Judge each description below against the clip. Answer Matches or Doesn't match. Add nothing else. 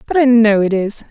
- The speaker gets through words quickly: Matches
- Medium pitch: Doesn't match